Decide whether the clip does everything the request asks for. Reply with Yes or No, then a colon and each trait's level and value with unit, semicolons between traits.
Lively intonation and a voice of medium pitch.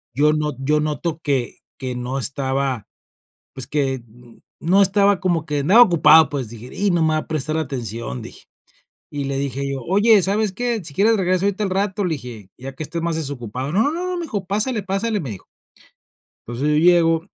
Yes: wide, 6.2 semitones; medium, 155 Hz